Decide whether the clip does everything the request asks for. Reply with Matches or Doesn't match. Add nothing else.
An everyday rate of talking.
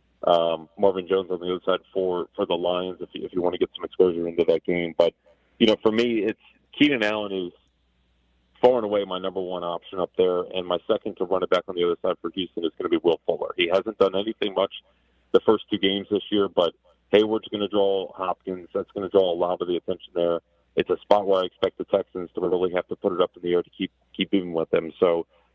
Doesn't match